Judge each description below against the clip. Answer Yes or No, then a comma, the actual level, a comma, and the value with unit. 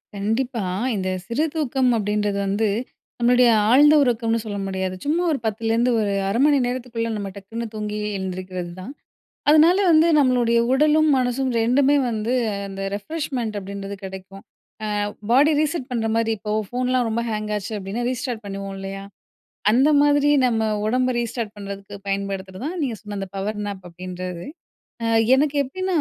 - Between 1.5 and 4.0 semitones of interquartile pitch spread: No, average, 4.5 semitones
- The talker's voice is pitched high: Yes, high, 225 Hz